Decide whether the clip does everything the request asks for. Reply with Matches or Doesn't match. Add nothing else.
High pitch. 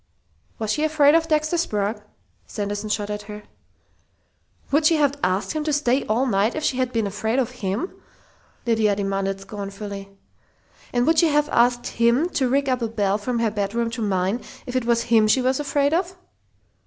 Matches